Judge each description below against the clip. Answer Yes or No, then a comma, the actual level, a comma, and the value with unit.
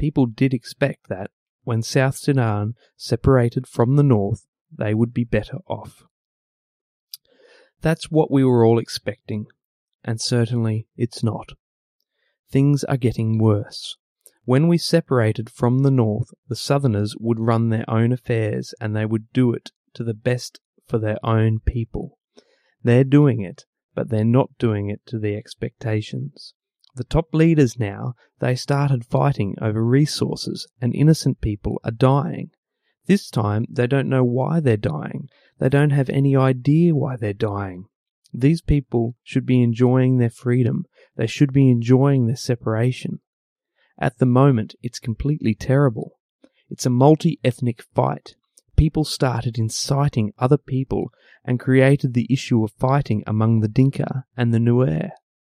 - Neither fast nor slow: Yes, average, 150 wpm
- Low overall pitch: Yes, low, 125 Hz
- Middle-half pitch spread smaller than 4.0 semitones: Yes, average, 3.4 semitones